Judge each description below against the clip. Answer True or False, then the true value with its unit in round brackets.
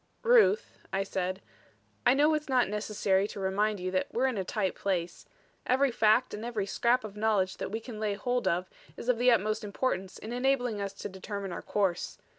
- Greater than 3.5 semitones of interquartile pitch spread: True (4.2 semitones)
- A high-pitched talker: True (210 Hz)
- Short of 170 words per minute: False (205 wpm)